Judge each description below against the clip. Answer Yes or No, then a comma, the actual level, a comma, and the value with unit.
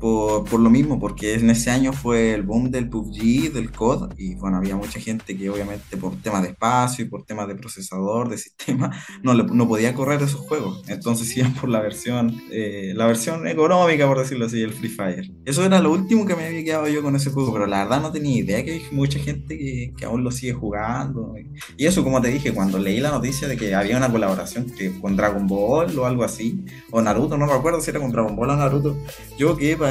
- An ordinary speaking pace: No, fast, 235 wpm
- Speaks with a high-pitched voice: No, low, 120 Hz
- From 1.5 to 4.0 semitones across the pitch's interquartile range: No, average, 4.7 semitones